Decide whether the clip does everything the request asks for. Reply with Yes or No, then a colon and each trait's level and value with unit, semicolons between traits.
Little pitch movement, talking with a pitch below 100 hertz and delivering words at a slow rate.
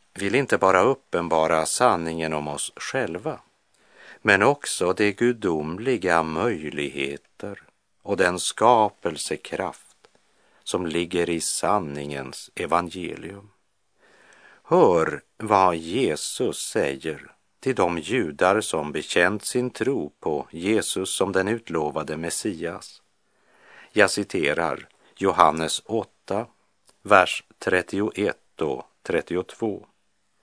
No: average, 4.2 semitones; very low, 85 Hz; slow, 90 wpm